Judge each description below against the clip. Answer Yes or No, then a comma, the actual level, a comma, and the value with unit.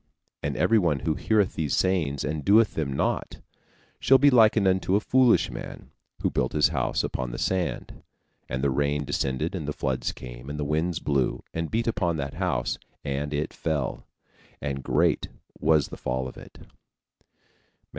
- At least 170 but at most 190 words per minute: Yes, average, 175 wpm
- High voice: No, very low, 75 Hz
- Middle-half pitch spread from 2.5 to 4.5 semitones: No, wide, 5.4 semitones